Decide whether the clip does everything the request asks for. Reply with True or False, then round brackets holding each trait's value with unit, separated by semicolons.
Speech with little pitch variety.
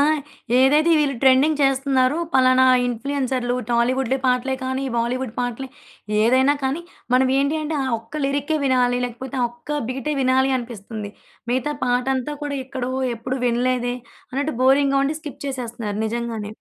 True (2.1 semitones)